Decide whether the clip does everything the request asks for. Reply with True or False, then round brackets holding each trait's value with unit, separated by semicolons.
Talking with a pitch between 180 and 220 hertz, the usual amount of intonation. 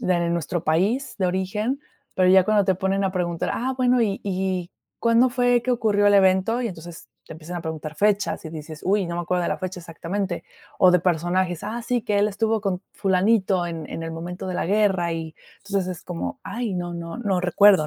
True (185 Hz; 3.2 semitones)